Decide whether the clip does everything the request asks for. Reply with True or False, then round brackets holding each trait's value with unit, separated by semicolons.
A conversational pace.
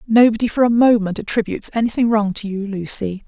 True (185 wpm)